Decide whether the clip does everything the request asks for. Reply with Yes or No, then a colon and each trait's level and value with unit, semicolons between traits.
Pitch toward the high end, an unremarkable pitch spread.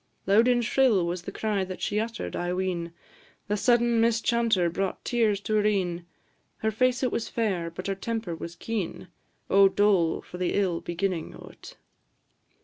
Yes: high, 200 Hz; average, 4.1 semitones